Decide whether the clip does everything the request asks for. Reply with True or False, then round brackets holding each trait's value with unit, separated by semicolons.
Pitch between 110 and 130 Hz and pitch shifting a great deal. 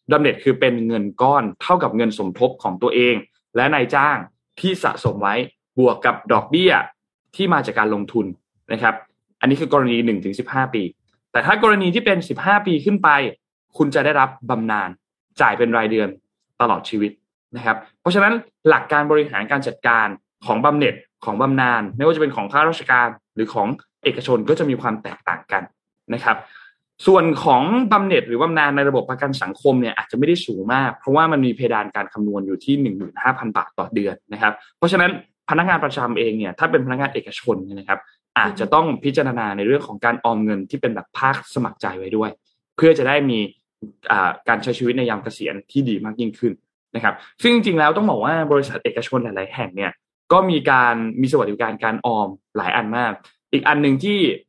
True (125 Hz; 5.7 semitones)